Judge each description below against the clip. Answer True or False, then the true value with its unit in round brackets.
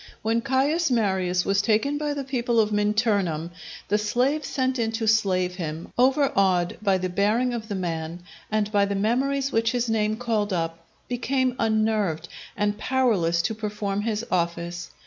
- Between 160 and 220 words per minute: True (165 wpm)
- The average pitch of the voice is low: False (215 Hz)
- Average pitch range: True (4.6 semitones)